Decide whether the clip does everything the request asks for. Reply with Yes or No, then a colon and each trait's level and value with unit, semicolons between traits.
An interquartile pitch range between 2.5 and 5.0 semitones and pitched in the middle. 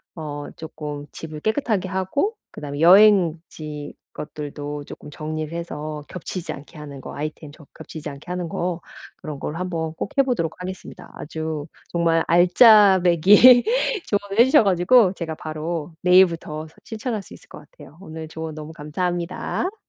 Yes: average, 3.6 semitones; medium, 165 Hz